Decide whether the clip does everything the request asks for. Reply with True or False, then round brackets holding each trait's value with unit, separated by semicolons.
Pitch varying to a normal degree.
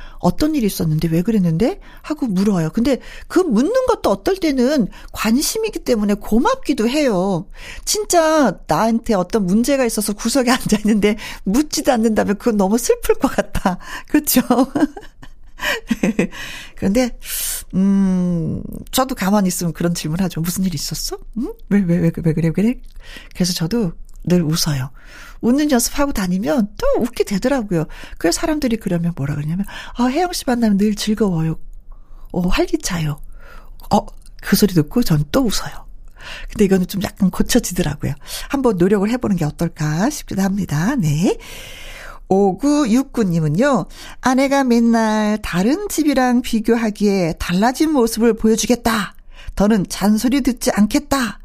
False (5.8 semitones)